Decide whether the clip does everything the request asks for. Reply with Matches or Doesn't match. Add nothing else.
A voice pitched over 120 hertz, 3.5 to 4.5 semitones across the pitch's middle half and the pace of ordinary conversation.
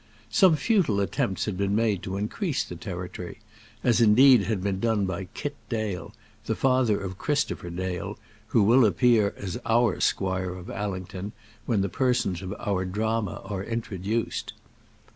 Doesn't match